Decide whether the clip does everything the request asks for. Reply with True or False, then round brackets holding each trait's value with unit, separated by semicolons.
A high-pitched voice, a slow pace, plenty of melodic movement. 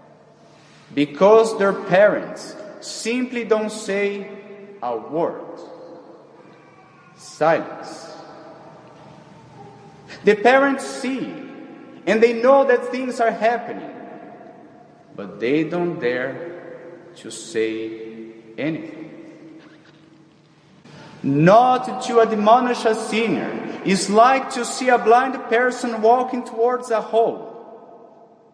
True (220 Hz; 90 wpm; 7.3 semitones)